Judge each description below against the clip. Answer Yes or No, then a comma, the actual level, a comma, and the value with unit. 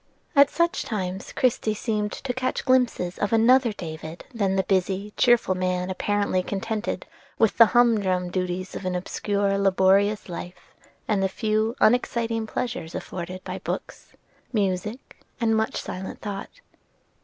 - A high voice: Yes, high, 205 Hz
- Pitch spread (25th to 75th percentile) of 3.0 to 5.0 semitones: Yes, average, 3.5 semitones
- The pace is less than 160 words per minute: Yes, average, 140 wpm